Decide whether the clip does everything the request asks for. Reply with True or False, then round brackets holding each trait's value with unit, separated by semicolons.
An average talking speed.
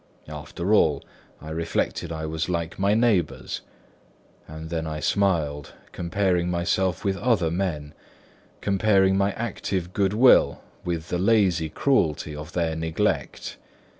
False (130 wpm)